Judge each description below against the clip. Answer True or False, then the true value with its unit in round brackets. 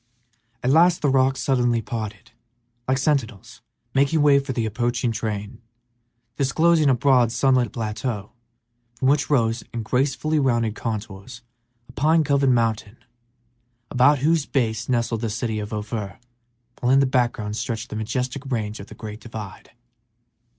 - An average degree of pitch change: True (3.6 semitones)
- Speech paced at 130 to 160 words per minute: True (150 wpm)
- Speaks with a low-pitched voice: True (120 Hz)